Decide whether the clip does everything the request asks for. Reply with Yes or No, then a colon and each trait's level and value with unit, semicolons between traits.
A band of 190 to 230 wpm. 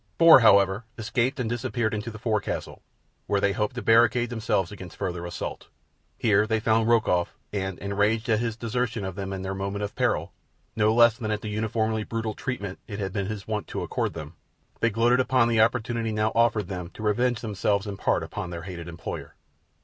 Yes: average, 200 wpm